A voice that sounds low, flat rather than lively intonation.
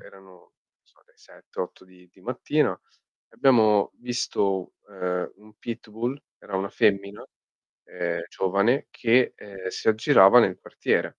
No: low, 100 Hz; average, 3.4 semitones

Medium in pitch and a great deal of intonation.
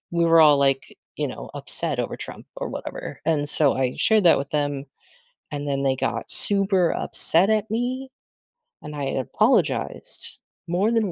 Yes: medium, 165 Hz; wide, 6.2 semitones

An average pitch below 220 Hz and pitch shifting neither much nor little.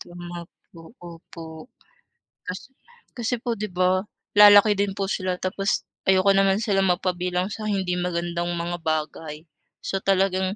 No: medium, 185 Hz; narrow, 2.2 semitones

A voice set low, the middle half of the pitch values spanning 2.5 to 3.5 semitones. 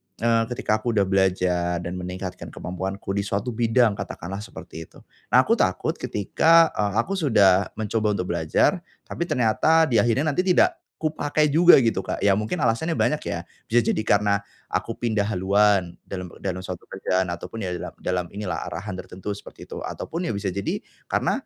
No: low, 105 Hz; average, 4.3 semitones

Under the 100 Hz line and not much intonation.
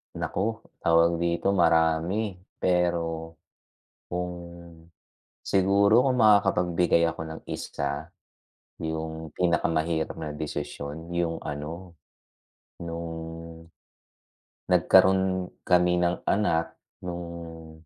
Yes: very low, 85 Hz; narrow, 1.9 semitones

